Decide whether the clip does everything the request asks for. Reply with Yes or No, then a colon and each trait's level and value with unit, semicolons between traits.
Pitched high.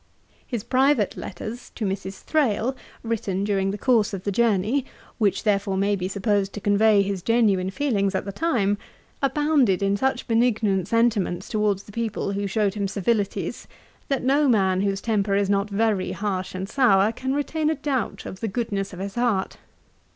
Yes: high, 205 Hz